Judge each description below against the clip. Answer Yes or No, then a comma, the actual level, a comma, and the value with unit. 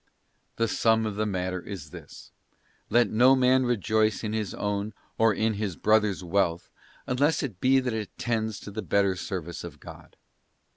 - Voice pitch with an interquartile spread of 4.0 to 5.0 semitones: No, narrow, 2.6 semitones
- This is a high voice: No, low, 110 Hz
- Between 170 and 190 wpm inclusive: Yes, average, 175 wpm